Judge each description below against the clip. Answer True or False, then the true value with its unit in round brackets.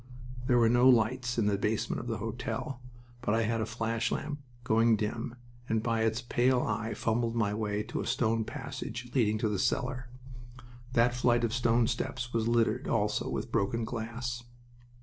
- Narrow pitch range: True (1.5 semitones)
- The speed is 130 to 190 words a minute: True (180 wpm)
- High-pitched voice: False (115 Hz)